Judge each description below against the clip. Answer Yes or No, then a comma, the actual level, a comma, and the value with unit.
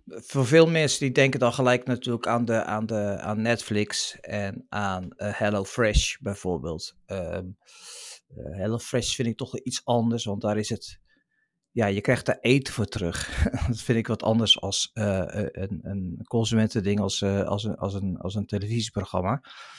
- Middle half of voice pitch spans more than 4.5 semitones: No, average, 3.4 semitones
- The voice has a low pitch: Yes, low, 110 Hz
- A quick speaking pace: No, average, 175 wpm